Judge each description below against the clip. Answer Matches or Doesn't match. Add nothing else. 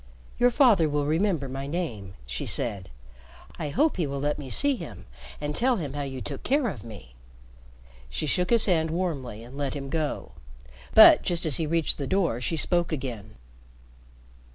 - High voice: Doesn't match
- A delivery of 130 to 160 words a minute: Doesn't match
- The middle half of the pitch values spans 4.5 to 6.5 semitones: Matches